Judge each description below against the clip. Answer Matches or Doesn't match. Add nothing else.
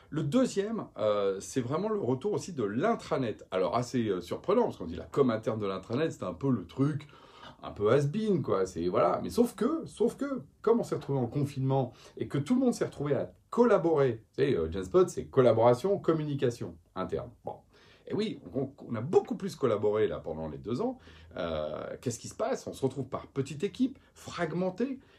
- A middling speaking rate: Matches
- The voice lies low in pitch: Doesn't match